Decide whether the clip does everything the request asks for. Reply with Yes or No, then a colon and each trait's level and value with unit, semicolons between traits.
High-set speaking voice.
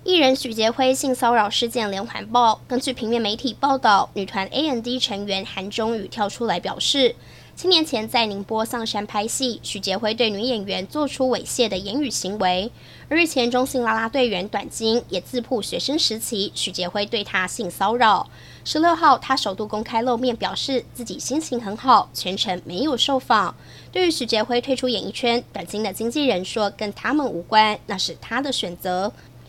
Yes: high, 230 Hz